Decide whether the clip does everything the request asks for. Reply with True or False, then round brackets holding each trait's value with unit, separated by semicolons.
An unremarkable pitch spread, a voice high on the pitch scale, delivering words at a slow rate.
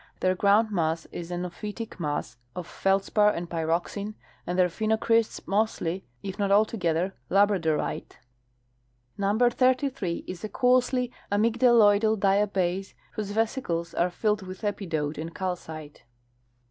True (3.7 semitones; 195 Hz; 120 wpm)